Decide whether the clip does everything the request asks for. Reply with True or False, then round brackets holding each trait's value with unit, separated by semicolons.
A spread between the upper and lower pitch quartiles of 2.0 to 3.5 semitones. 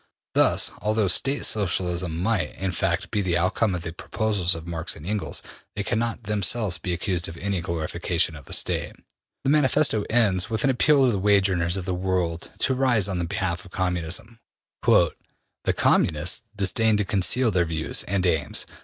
False (4.0 semitones)